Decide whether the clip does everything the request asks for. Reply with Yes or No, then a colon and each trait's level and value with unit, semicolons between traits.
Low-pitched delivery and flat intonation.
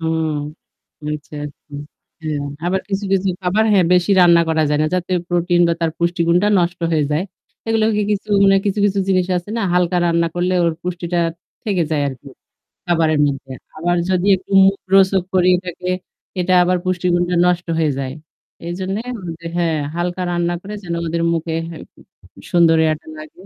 No: medium, 175 Hz; narrow, 2.0 semitones